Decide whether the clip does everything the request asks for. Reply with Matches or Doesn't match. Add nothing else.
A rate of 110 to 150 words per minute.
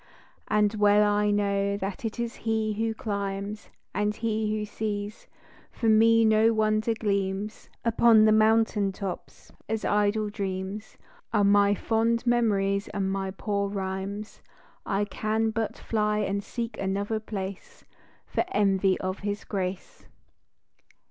Matches